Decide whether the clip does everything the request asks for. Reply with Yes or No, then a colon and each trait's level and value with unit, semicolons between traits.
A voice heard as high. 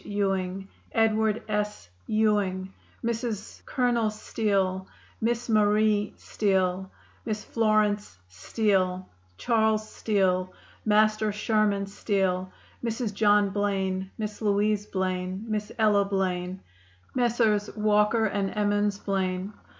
Yes: high, 205 Hz